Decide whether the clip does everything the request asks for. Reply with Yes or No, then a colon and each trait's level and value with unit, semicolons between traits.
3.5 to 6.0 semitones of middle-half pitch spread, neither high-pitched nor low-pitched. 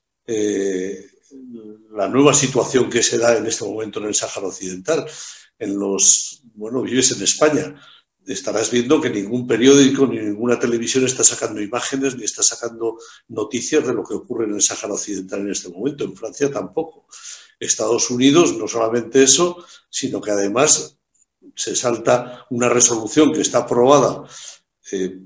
No: average, 4.3 semitones; low, 120 Hz